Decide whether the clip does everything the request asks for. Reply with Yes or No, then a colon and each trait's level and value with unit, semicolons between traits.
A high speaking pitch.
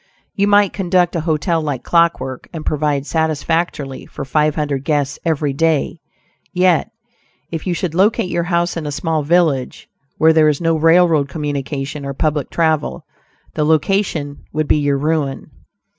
No: medium, 155 Hz